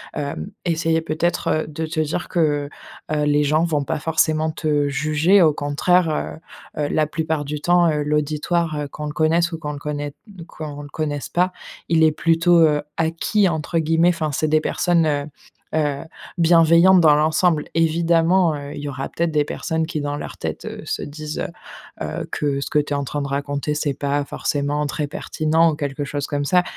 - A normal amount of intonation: No, narrow, 2.0 semitones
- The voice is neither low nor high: Yes, medium, 155 Hz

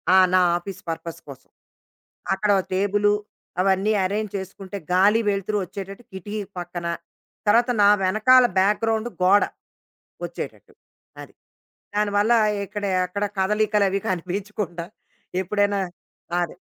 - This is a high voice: Yes, high, 200 Hz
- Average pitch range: No, narrow, 2.0 semitones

